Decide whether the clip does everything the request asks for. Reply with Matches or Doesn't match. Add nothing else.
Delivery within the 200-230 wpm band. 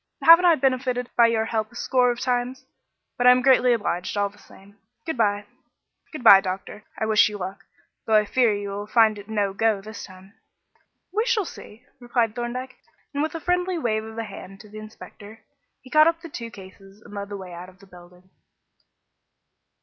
Matches